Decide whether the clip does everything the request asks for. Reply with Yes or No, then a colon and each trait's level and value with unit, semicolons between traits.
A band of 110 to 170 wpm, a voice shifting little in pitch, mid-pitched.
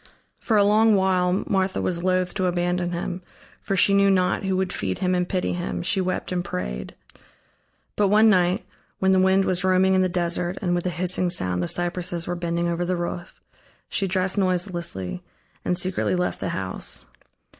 No: average, 190 wpm; narrow, 1.4 semitones; medium, 180 Hz